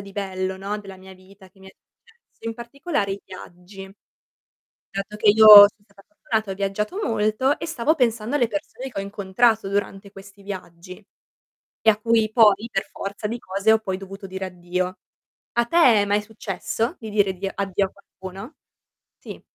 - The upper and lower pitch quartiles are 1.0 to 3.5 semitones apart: Yes, narrow, 2.5 semitones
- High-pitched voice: Yes, high, 200 Hz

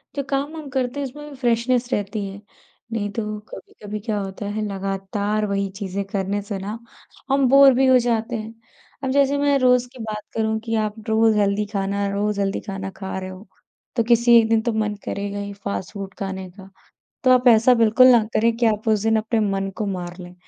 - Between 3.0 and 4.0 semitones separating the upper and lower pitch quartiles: Yes, average, 3.3 semitones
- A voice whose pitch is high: Yes, high, 215 Hz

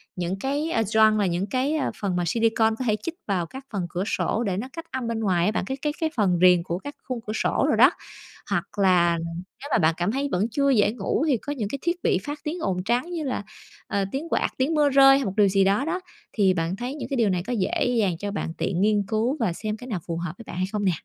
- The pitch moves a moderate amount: No, wide, 6.3 semitones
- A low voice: No, high, 215 Hz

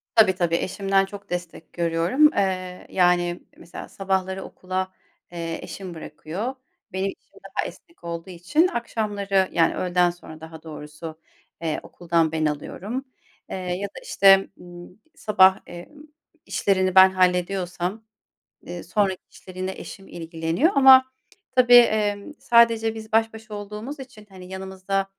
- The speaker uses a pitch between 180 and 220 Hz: Yes, high, 190 Hz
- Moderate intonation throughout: Yes, average, 3.2 semitones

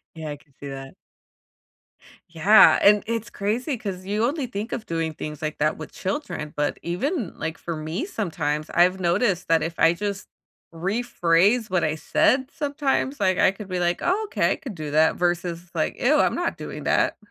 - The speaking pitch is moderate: Yes, medium, 180 Hz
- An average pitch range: No, wide, 5.9 semitones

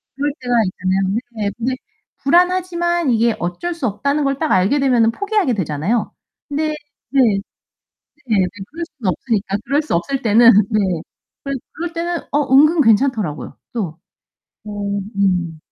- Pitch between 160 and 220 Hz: No, high, 245 Hz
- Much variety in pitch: Yes, wide, 6.9 semitones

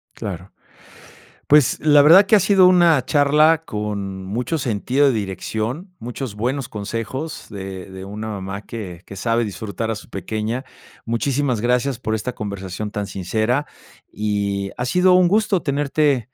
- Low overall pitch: Yes, low, 115 Hz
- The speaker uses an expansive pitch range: Yes, wide, 6.1 semitones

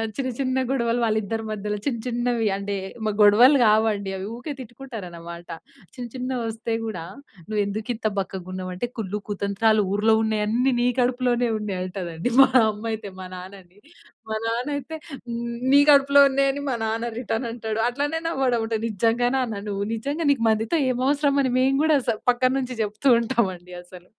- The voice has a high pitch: Yes, high, 225 Hz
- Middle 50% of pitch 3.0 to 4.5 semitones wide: Yes, average, 3.7 semitones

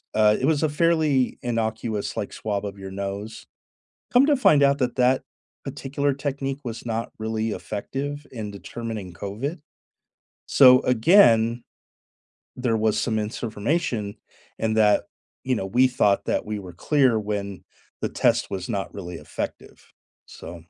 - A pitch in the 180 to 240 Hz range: No, low, 115 Hz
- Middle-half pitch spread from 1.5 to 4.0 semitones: No, average, 4.6 semitones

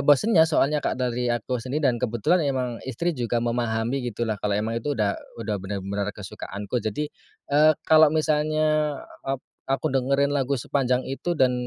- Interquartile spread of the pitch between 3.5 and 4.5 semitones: Yes, average, 4.2 semitones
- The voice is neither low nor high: No, low, 130 Hz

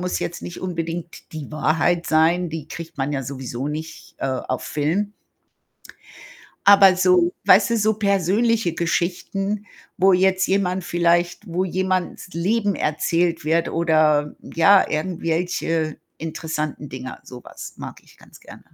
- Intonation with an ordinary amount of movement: Yes, average, 3.1 semitones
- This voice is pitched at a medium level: Yes, medium, 170 Hz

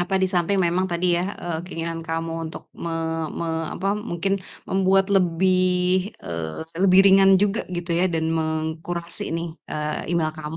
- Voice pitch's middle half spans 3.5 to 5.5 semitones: No, narrow, 2.5 semitones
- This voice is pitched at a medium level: Yes, medium, 170 Hz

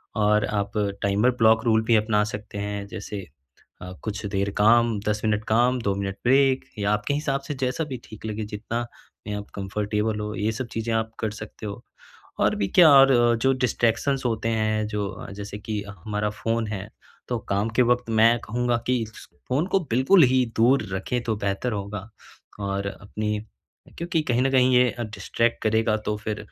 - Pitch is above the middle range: No, low, 110 Hz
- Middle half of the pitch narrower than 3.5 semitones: Yes, average, 2.8 semitones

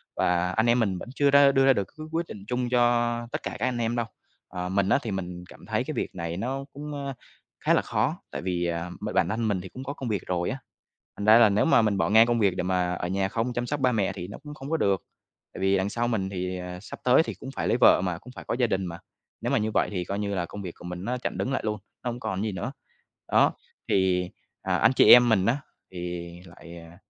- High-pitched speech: No, low, 105 Hz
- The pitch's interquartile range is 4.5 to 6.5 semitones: Yes, average, 5.2 semitones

